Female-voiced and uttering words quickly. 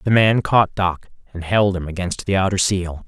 No: male; fast, 215 wpm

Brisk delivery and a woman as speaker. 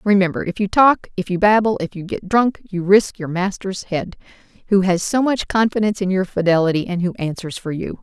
Yes: fast, 215 wpm; female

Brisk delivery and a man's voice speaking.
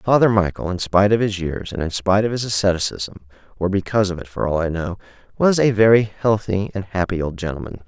Yes: fast, 220 wpm; male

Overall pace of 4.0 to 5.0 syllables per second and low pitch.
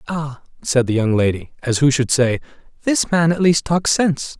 No: 4.8 syllables/s; medium, 145 Hz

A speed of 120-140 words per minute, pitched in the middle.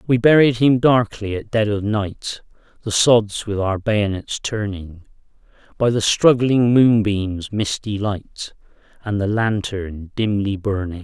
No: slow, 135 wpm; low, 105 Hz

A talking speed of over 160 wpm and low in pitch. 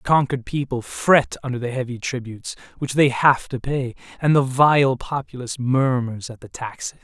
Yes: average, 180 wpm; low, 130 Hz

